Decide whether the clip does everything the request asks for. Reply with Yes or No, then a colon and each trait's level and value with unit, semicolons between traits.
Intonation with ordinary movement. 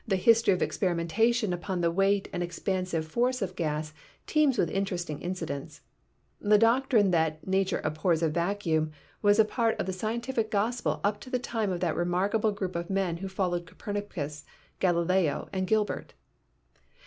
Yes: average, 3.8 semitones